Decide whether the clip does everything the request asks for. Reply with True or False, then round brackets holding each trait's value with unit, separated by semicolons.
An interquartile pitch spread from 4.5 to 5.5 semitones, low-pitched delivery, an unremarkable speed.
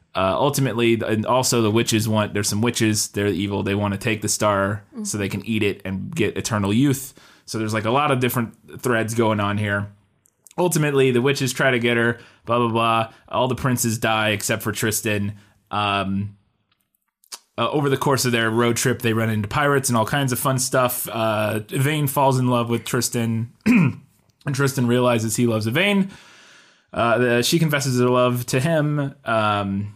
False (3.7 semitones; 115 Hz; 190 wpm)